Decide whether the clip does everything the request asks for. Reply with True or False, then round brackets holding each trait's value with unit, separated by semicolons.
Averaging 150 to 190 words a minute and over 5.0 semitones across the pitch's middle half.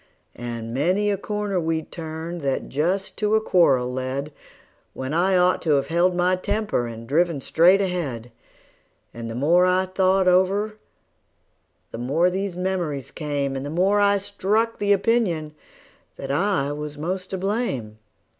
True (165 wpm; 5.4 semitones)